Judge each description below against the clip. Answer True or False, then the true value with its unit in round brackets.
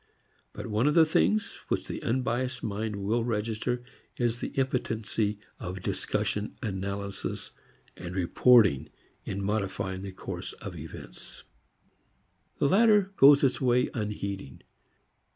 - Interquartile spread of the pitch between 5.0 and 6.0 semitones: False (4.3 semitones)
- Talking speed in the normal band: False (120 wpm)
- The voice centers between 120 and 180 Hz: False (110 Hz)